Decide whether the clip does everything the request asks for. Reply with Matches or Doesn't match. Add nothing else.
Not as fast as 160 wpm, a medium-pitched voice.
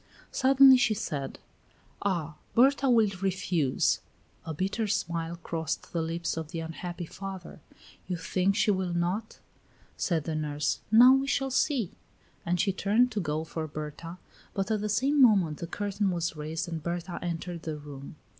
Doesn't match